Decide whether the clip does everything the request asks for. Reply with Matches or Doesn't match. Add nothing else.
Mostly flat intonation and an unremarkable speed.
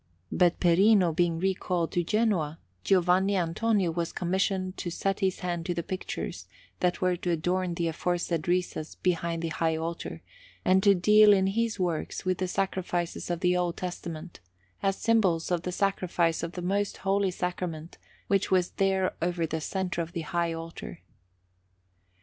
Matches